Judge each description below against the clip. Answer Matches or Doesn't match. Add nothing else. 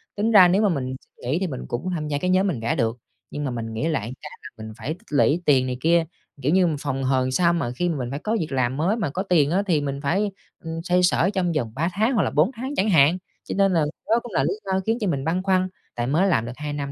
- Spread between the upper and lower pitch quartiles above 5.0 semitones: Matches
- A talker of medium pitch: Matches